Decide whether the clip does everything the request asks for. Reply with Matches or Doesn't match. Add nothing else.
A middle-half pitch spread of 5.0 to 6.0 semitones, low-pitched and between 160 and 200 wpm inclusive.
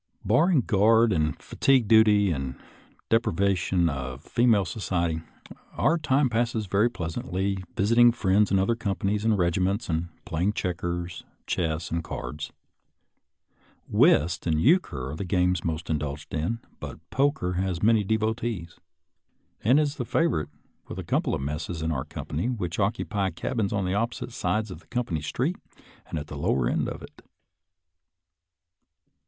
Doesn't match